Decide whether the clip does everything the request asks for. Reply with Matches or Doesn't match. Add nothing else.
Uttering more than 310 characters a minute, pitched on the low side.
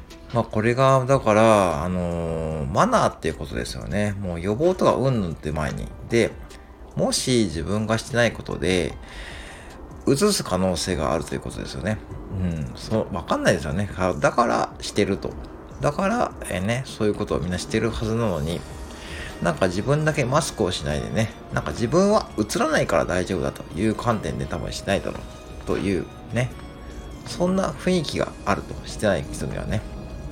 Matches